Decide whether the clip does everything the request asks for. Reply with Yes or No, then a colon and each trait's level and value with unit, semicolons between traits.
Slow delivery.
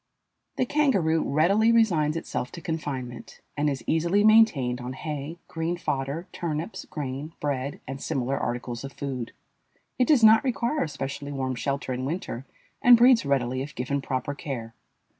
No: average, 160 wpm